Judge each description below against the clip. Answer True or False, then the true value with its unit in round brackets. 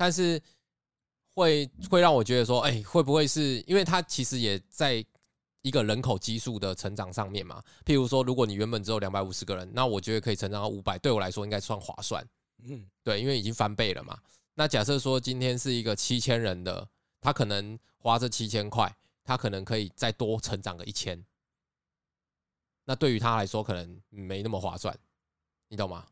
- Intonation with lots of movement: False (4.2 semitones)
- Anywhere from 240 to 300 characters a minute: True (295 characters per minute)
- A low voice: True (110 Hz)